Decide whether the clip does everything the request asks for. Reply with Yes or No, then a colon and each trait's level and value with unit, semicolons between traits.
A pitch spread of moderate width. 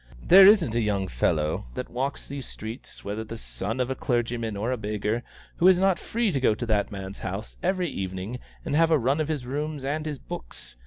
No: wide, 6.5 semitones